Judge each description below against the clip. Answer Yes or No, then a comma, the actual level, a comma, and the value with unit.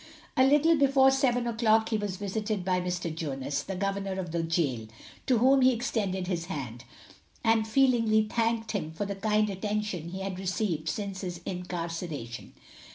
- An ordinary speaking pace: Yes, average, 165 wpm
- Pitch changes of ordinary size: Yes, average, 4.4 semitones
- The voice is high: Yes, high, 195 Hz